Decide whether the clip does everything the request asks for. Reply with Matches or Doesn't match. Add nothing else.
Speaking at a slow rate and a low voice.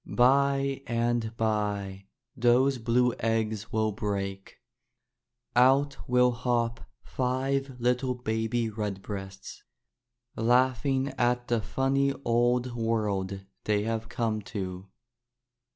Matches